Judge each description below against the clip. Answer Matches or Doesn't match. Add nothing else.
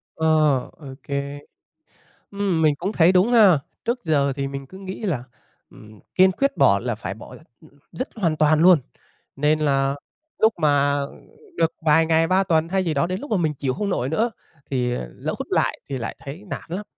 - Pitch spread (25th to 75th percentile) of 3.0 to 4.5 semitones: Doesn't match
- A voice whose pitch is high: Doesn't match